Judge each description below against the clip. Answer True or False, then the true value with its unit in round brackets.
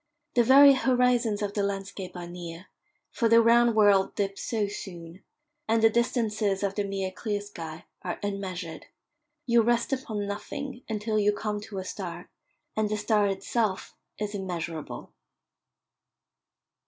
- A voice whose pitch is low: False (205 Hz)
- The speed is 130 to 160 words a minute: True (145 wpm)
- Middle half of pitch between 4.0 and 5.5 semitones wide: False (2.8 semitones)